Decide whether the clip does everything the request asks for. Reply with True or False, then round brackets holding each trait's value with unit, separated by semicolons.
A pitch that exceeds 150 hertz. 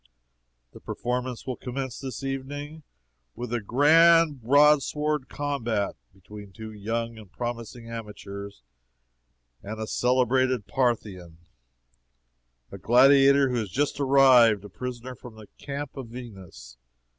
False (125 Hz)